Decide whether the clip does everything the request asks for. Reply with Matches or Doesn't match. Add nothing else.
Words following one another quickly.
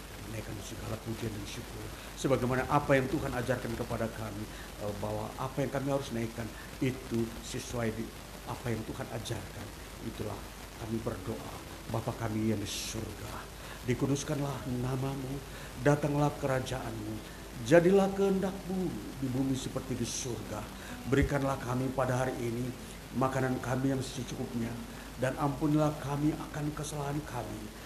Doesn't match